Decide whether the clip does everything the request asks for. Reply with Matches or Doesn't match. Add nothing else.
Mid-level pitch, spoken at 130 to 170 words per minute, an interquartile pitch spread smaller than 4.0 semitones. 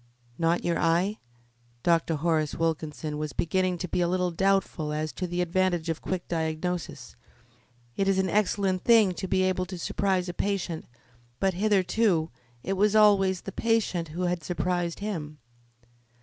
Matches